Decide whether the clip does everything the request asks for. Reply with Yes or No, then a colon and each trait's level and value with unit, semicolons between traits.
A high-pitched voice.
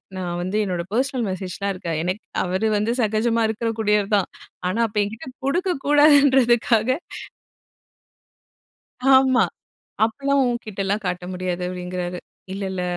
Yes: high, 210 Hz